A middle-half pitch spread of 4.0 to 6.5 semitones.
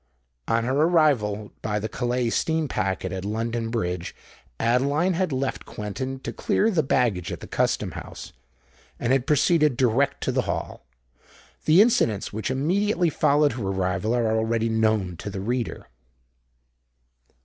Yes: wide, 5.6 semitones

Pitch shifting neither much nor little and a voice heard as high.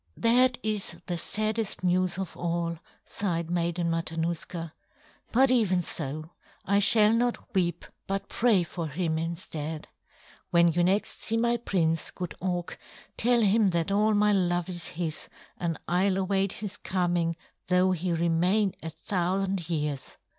No: average, 3.2 semitones; medium, 180 Hz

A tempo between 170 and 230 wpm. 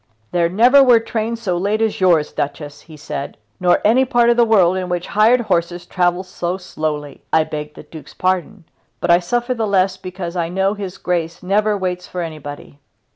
Yes: average, 195 wpm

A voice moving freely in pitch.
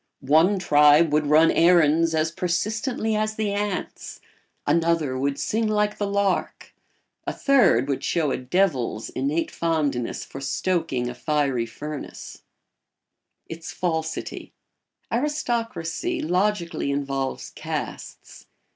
Yes: wide, 5.8 semitones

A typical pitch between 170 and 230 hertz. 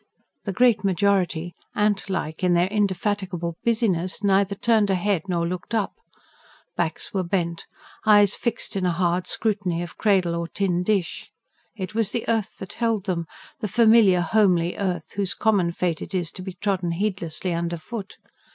Yes: high, 190 Hz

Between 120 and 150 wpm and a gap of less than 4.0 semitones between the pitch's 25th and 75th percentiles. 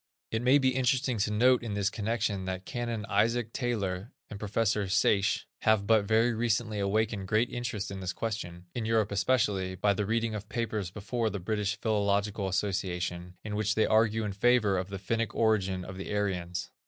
No: average, 185 wpm; narrow, 2.6 semitones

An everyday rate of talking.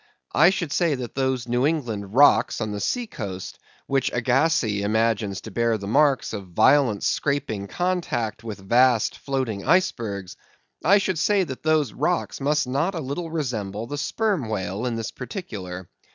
Yes: average, 160 wpm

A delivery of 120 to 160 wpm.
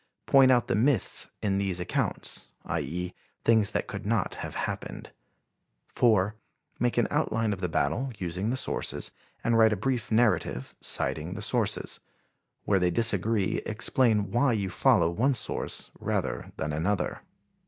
Yes: average, 155 wpm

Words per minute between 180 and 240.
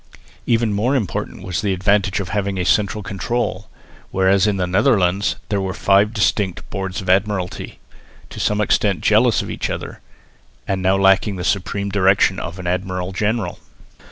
No: average, 165 wpm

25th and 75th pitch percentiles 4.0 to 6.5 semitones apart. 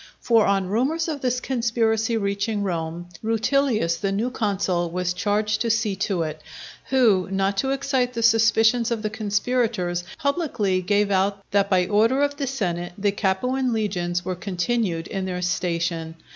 Yes: average, 4.3 semitones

